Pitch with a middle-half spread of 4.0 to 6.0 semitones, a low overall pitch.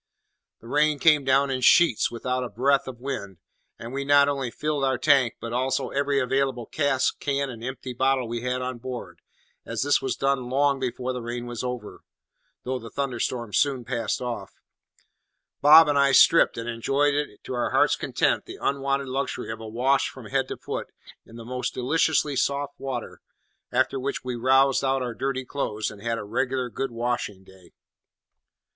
No: narrow, 2.4 semitones; low, 130 Hz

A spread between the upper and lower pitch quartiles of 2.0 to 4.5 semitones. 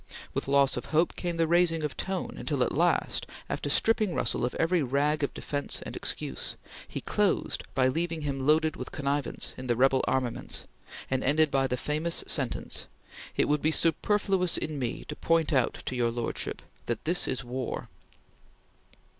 Yes: average, 3.9 semitones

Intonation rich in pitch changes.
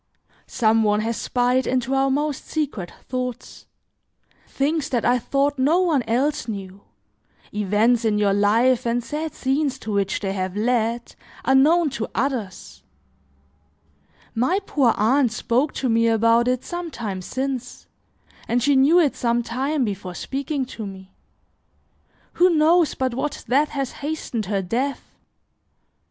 No: average, 4.1 semitones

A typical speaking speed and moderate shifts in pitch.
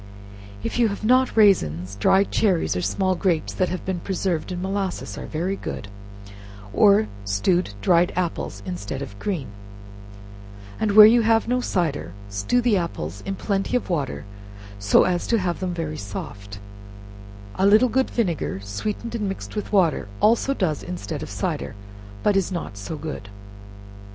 No: average, 160 wpm; wide, 6.9 semitones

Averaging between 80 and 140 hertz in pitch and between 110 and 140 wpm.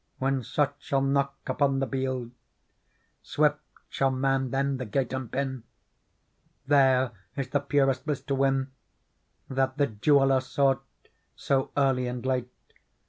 Yes: low, 135 Hz; slow, 135 wpm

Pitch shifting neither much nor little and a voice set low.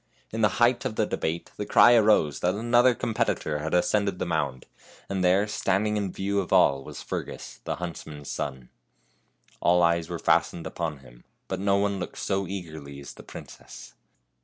Yes: average, 4.6 semitones; very low, 90 Hz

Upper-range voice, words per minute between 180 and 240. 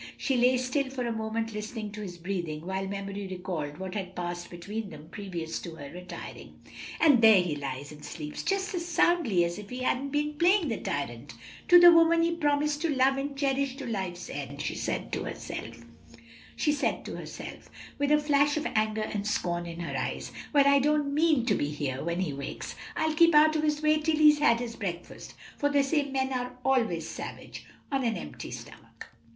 Yes: high, 230 Hz; average, 200 wpm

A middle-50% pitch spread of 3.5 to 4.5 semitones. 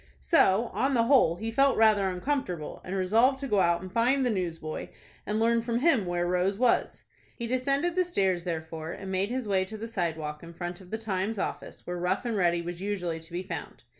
No: average, 5.0 semitones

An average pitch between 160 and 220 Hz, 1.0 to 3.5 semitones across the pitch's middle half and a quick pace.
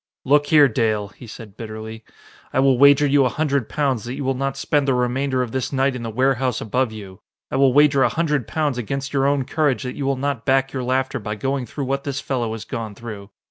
No: low, 130 Hz; average, 3.0 semitones; fast, 240 wpm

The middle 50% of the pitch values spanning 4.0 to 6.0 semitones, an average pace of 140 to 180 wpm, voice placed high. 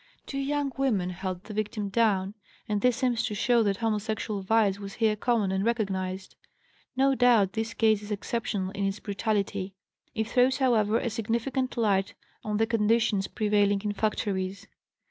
No: average, 2.7 semitones; average, 165 wpm; high, 215 Hz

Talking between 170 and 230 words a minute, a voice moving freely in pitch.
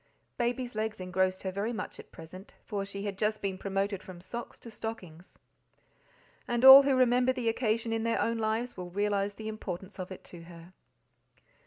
No: average, 185 wpm; average, 3.6 semitones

